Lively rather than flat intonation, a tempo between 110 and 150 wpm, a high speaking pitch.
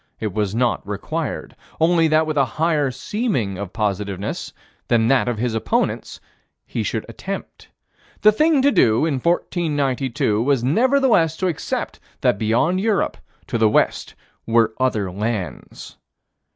No: wide, 7.2 semitones; average, 140 wpm; low, 130 Hz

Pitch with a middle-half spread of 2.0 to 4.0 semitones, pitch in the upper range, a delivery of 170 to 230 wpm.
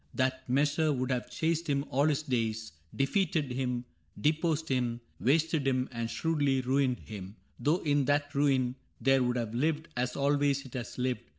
No: average, 2.8 semitones; low, 135 Hz; average, 175 wpm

